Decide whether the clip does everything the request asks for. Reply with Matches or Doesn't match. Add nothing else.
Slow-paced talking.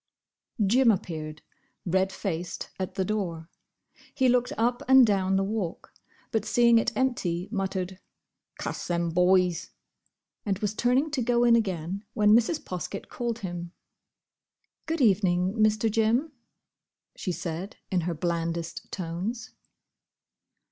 Matches